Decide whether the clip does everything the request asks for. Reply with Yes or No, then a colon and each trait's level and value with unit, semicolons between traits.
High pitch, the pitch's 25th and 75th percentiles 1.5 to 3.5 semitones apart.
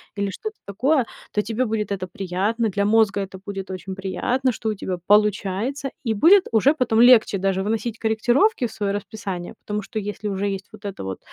Yes: high, 210 Hz; average, 2.9 semitones